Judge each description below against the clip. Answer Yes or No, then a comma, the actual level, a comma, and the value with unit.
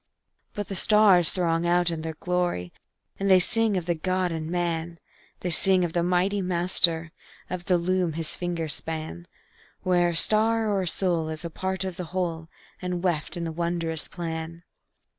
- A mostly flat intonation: Yes, narrow, 2.1 semitones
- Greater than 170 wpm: Yes, average, 180 wpm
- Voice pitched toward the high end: No, medium, 175 Hz